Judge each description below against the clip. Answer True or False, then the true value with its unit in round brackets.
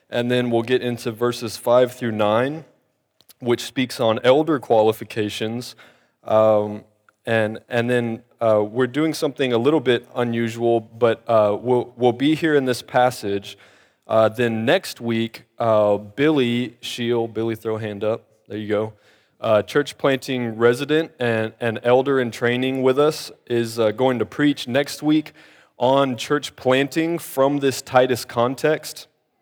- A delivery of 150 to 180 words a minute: True (155 wpm)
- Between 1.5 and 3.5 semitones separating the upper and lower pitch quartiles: True (3.0 semitones)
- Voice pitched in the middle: False (120 Hz)